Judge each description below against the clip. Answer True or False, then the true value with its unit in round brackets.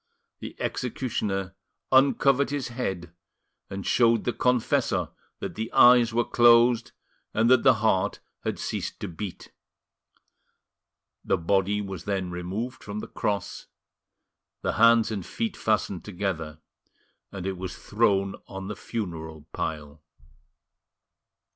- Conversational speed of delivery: False (120 wpm)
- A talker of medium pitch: False (105 Hz)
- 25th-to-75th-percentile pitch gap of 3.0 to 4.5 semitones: True (4.0 semitones)